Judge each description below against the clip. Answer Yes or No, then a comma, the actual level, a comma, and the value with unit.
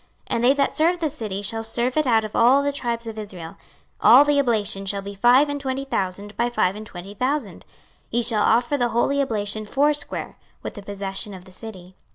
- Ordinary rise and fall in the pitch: Yes, average, 5.0 semitones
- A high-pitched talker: Yes, high, 230 Hz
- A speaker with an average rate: No, fast, 220 wpm